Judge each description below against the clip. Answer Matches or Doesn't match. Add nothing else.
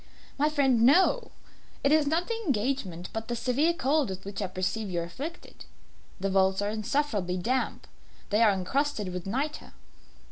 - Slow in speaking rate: Doesn't match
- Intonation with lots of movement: Matches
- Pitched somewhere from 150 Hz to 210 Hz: Doesn't match